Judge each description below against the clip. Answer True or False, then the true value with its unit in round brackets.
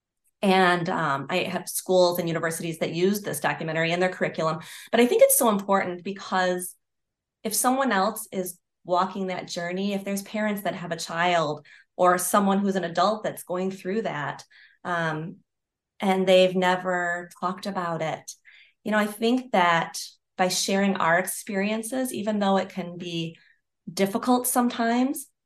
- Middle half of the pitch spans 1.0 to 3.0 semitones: True (2.6 semitones)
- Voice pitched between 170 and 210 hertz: True (185 Hz)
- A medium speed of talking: True (160 wpm)